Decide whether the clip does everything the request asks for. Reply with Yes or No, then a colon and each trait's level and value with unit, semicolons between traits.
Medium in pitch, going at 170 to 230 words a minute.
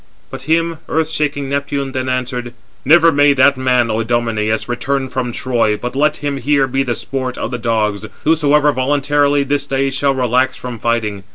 No: low, 130 Hz; average, 180 wpm